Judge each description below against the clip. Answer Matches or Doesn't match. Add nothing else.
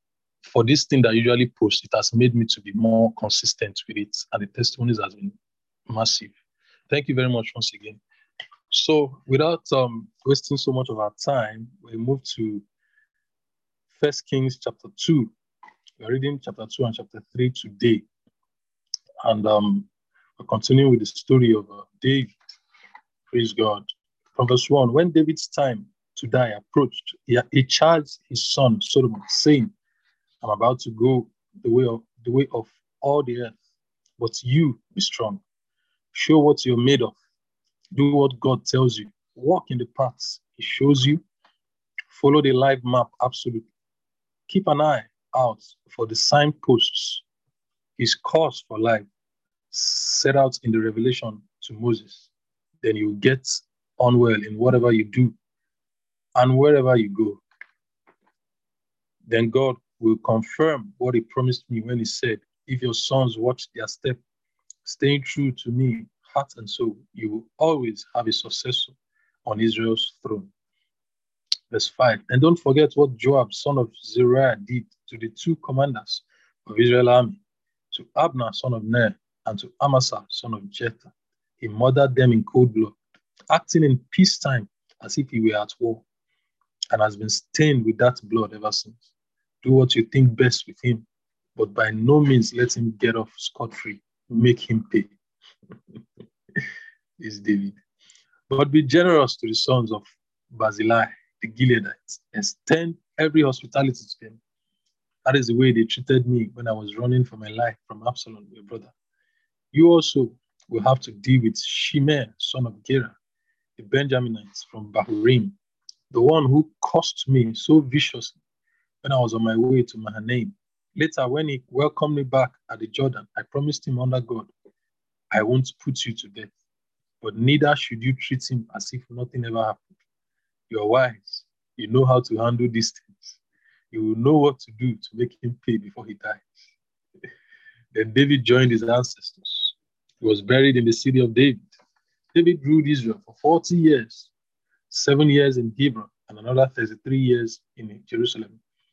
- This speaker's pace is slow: Doesn't match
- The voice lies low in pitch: Matches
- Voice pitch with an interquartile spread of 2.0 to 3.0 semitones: Doesn't match